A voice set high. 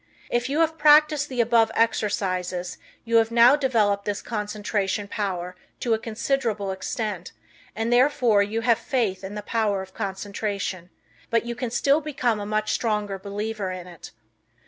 Yes: high, 215 Hz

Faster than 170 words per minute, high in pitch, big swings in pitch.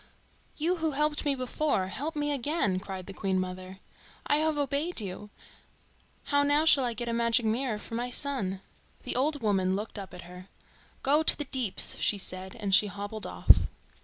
Yes: average, 190 wpm; high, 235 Hz; wide, 6.9 semitones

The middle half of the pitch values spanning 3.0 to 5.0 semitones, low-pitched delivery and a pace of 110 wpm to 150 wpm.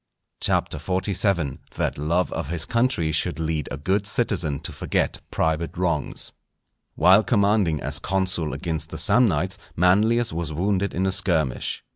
Yes: average, 4.0 semitones; very low, 90 Hz; average, 140 wpm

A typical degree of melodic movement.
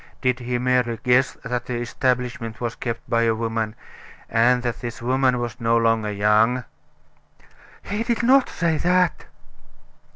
No: narrow, 1.9 semitones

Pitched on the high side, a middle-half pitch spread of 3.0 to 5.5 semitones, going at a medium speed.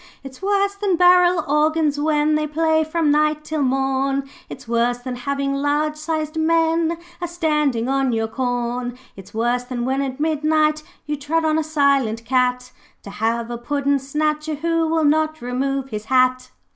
Yes: very high, 290 Hz; average, 3.6 semitones; average, 170 wpm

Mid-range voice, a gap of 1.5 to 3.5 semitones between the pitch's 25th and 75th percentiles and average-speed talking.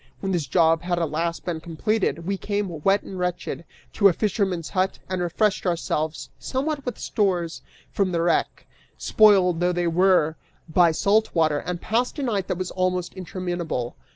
Yes: medium, 180 Hz; average, 2.8 semitones; average, 175 wpm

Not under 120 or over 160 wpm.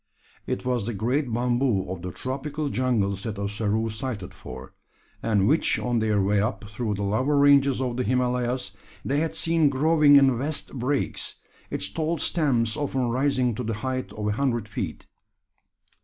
No: average, 170 wpm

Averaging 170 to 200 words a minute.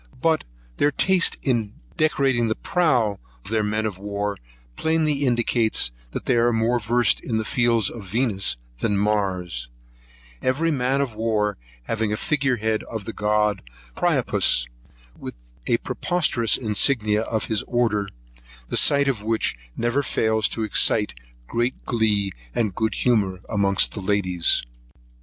No: average, 145 wpm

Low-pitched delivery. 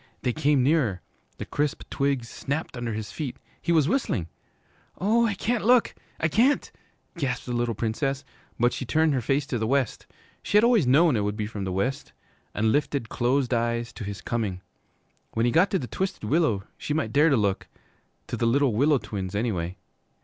Yes: low, 130 Hz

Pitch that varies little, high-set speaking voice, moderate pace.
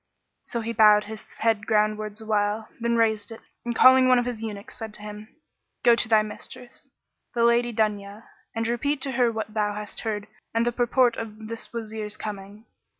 Yes: narrow, 1.8 semitones; high, 220 Hz; average, 190 wpm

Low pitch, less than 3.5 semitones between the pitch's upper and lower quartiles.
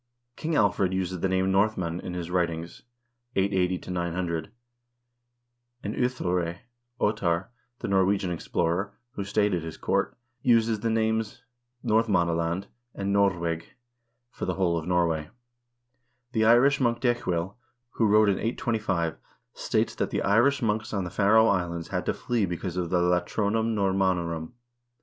No: very low, 95 Hz; average, 3.9 semitones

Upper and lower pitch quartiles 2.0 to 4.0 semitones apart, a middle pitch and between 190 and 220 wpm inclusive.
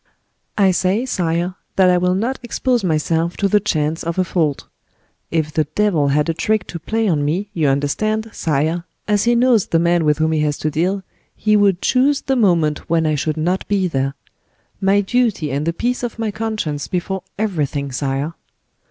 No: average, 5.2 semitones; medium, 175 Hz; average, 195 wpm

